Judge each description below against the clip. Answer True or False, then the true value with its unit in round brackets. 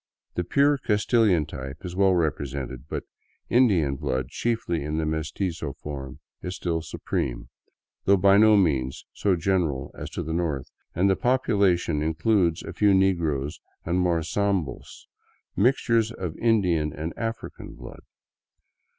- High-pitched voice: False (85 Hz)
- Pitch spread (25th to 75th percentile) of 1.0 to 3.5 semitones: False (4.8 semitones)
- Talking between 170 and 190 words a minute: False (140 wpm)